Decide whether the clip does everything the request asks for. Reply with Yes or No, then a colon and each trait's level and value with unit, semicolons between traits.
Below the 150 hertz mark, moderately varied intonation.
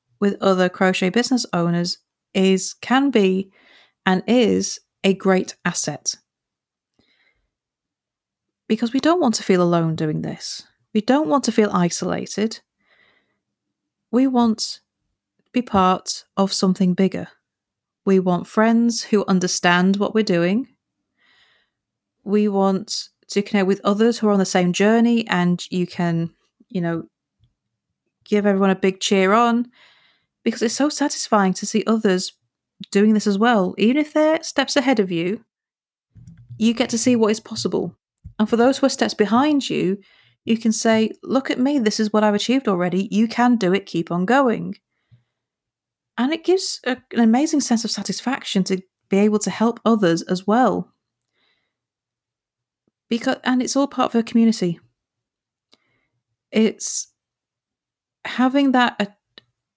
No: high, 210 Hz; average, 4.2 semitones